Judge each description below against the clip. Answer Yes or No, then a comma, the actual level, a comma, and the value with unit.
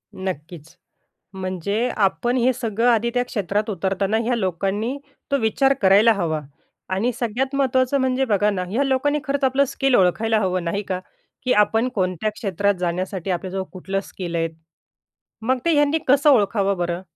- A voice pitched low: No, high, 210 Hz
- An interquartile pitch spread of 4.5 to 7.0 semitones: Yes, average, 5.2 semitones